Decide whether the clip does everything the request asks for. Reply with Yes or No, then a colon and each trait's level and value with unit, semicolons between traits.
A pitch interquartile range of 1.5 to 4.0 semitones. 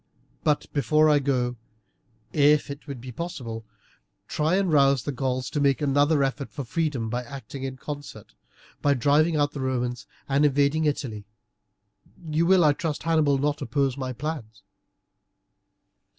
Yes: narrow, 2.6 semitones